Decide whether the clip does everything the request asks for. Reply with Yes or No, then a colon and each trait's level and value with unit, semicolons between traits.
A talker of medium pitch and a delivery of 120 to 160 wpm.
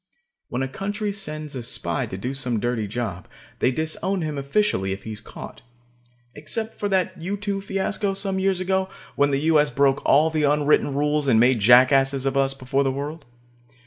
No: medium, 145 Hz; average, 190 wpm